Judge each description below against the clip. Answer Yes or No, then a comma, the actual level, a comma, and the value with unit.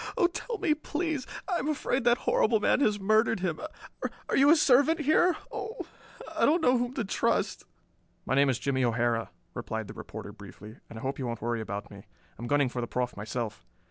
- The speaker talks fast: Yes, fast, 210 wpm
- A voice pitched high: Yes, high, 195 Hz